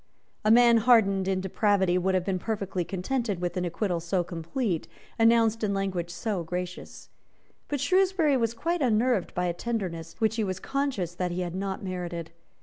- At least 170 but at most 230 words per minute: Yes, average, 175 wpm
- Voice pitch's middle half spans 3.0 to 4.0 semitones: No, average, 4.4 semitones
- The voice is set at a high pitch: Yes, high, 195 Hz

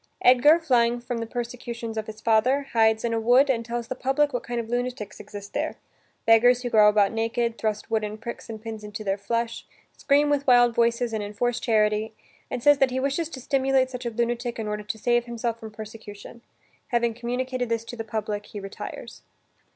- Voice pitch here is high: Yes, high, 235 Hz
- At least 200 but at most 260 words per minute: Yes, fast, 205 wpm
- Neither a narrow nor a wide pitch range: No, narrow, 2.1 semitones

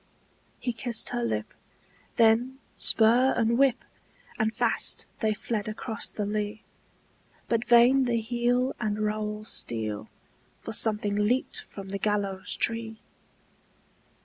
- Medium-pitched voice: No, high, 220 Hz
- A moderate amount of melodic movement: No, narrow, 2.3 semitones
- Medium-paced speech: No, slow, 120 wpm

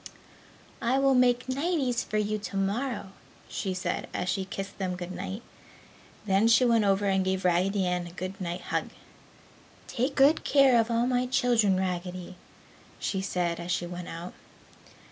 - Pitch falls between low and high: No, high, 195 Hz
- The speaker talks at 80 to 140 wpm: No, average, 165 wpm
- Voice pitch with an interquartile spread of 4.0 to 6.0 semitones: Yes, average, 4.8 semitones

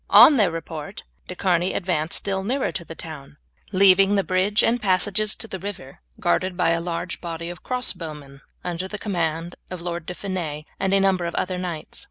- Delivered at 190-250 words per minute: Yes, fast, 205 wpm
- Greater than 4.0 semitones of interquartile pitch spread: No, average, 2.8 semitones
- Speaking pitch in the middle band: Yes, medium, 180 Hz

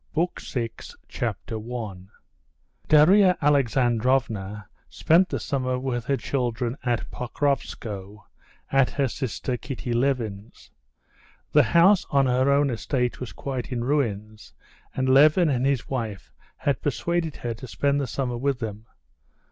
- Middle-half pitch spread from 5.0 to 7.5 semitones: No, average, 3.4 semitones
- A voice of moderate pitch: No, low, 130 Hz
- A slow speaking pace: Yes, slow, 130 wpm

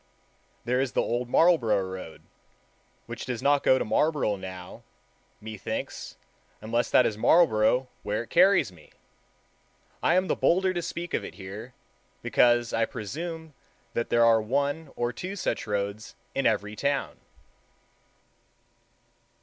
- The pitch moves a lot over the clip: Yes, wide, 6.0 semitones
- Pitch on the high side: No, low, 120 Hz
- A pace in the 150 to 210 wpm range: No, average, 140 wpm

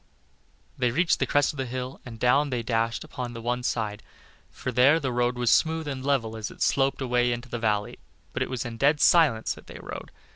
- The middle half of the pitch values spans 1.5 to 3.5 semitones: Yes, average, 2.9 semitones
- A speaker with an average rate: No, fast, 225 wpm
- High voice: No, low, 125 Hz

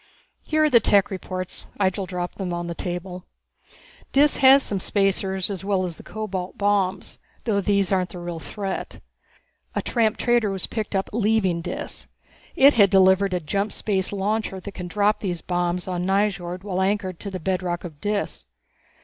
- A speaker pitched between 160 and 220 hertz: Yes, high, 190 Hz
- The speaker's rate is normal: Yes, average, 175 wpm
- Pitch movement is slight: Yes, narrow, 2.3 semitones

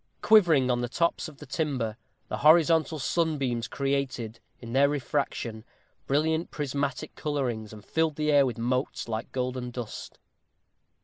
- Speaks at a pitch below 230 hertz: Yes, medium, 140 Hz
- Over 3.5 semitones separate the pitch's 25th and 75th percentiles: Yes, average, 3.9 semitones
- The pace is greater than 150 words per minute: No, average, 140 wpm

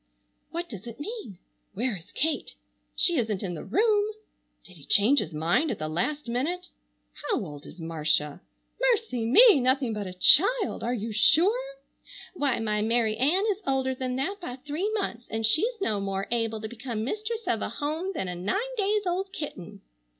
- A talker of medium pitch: No, very high, 250 Hz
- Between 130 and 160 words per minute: No, average, 185 wpm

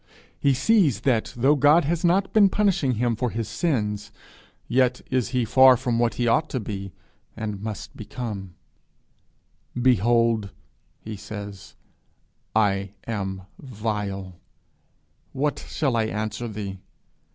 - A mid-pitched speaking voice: No, low, 115 Hz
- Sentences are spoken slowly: Yes, slow, 130 wpm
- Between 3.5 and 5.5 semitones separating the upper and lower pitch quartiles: Yes, average, 4.0 semitones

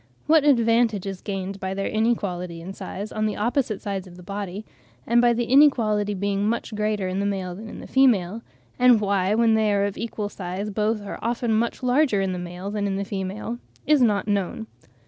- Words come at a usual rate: No, fast, 210 wpm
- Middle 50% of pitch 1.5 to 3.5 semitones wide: Yes, average, 2.9 semitones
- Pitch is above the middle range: Yes, high, 205 Hz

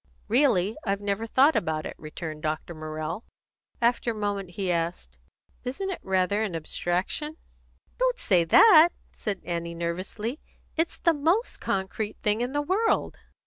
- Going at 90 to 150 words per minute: Yes, average, 145 wpm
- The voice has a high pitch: Yes, high, 205 Hz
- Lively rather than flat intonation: Yes, wide, 8.0 semitones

